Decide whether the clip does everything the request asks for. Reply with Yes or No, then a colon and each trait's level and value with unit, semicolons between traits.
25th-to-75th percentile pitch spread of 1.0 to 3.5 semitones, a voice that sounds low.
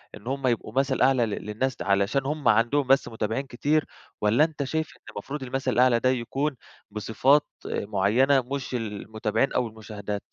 No: average, 4.0 semitones; low, 125 Hz